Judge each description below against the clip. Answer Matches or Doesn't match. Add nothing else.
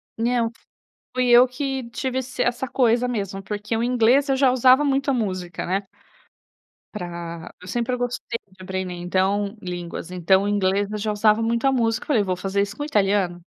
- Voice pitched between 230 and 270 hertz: Doesn't match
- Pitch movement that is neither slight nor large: Matches